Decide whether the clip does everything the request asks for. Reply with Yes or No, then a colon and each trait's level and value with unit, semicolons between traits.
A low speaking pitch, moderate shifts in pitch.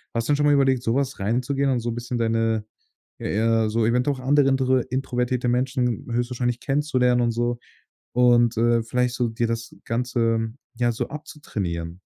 No: low, 120 Hz; narrow, 2.1 semitones